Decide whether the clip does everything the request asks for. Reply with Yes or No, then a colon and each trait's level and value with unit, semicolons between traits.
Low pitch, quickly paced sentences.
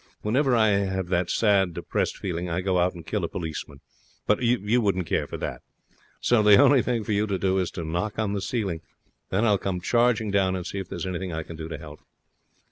Yes: very low, 95 Hz; fast, 230 wpm